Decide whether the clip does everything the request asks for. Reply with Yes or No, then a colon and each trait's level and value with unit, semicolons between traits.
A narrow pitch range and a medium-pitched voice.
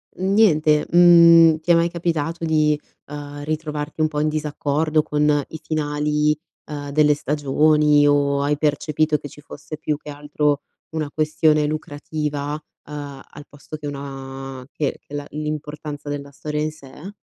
Yes: narrow, 1.1 semitones; medium, 150 Hz